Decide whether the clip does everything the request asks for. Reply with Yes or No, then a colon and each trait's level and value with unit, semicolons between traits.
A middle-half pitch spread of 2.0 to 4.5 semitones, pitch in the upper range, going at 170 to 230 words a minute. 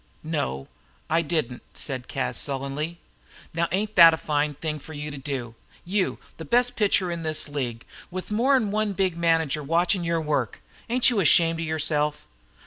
No: average, 3.7 semitones; medium, 160 Hz; average, 175 wpm